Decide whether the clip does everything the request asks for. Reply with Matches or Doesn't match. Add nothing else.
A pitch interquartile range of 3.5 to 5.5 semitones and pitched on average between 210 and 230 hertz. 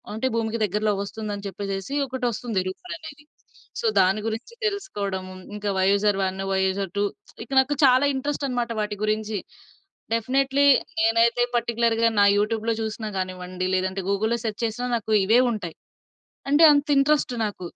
Matches